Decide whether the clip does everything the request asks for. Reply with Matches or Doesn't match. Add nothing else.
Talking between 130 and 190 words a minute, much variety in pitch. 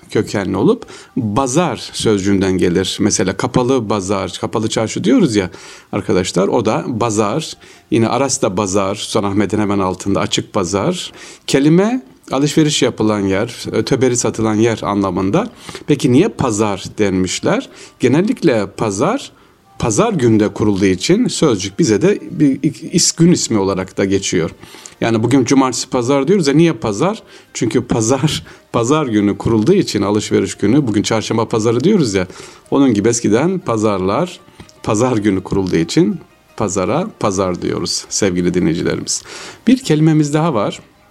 Matches